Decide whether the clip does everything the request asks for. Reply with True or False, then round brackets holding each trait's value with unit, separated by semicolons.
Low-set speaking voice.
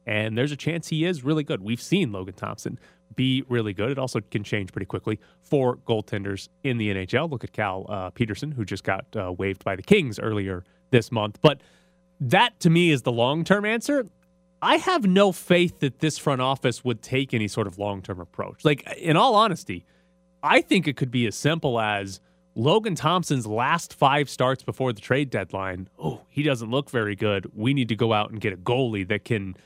True (125 Hz)